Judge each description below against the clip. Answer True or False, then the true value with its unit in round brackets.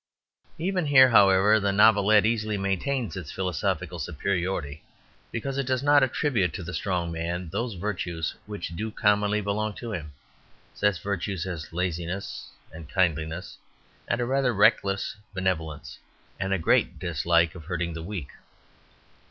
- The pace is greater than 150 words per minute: False (140 wpm)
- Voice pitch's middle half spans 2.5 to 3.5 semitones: False (4.0 semitones)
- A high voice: False (95 Hz)